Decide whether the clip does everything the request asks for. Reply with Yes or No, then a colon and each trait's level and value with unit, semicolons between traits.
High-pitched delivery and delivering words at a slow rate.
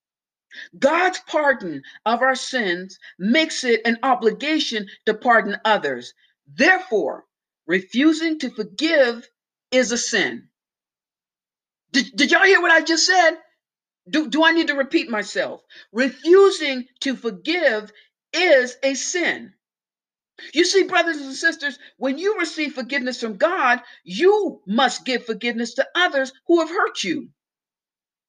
Yes: very high, 275 Hz; slow, 130 wpm